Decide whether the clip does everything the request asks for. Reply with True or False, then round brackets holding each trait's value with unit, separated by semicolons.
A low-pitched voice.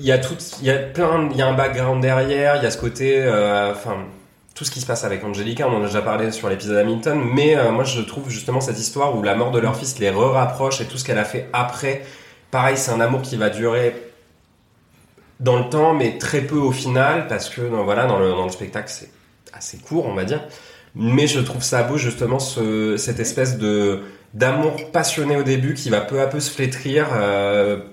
True (125 Hz)